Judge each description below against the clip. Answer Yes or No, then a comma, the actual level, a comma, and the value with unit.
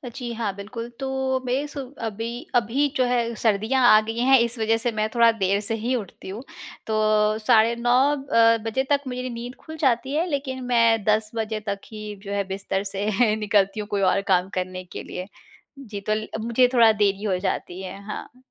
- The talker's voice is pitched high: Yes, high, 225 Hz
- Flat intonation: No, average, 3.2 semitones